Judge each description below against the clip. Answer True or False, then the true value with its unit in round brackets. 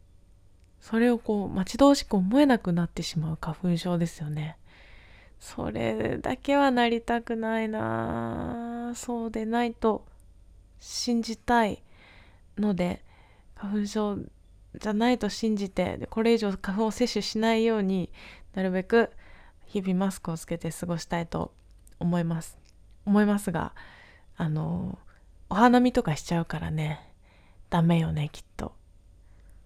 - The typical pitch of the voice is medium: True (175 Hz)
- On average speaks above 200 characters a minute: True (260 characters per minute)